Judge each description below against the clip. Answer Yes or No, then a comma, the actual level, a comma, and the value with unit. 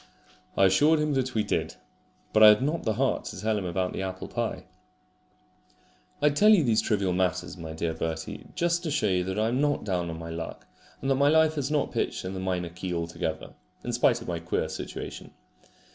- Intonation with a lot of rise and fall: Yes, wide, 7.8 semitones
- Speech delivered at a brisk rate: Yes, fast, 220 wpm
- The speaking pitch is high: No, low, 105 Hz